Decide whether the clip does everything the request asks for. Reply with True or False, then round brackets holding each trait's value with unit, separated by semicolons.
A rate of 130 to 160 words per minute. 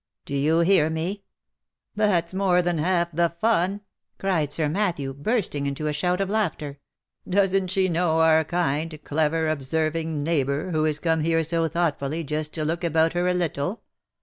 False (175 wpm)